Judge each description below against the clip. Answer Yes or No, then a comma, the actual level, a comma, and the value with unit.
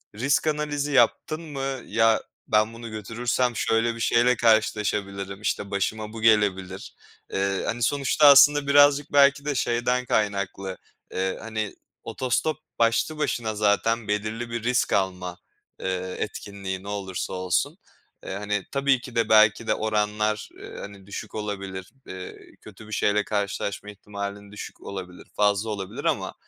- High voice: No, low, 110 Hz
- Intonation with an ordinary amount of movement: Yes, average, 3.2 semitones